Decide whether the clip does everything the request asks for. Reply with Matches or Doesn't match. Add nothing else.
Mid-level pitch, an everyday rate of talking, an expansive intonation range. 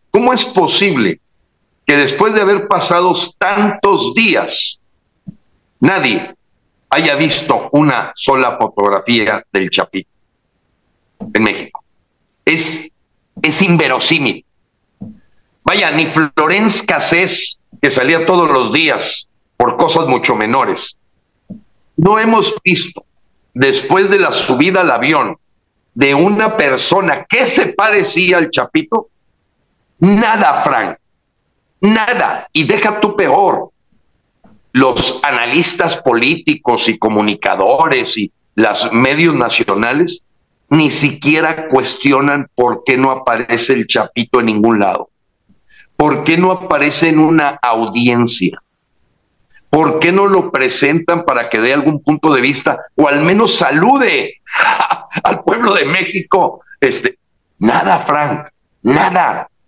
Doesn't match